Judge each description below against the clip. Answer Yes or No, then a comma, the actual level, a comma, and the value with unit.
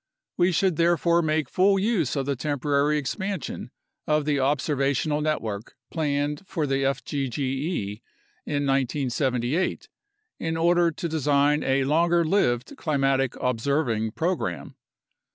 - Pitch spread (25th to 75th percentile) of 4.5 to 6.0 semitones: No, average, 3.3 semitones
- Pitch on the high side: No, medium, 145 Hz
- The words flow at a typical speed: No, slow, 115 wpm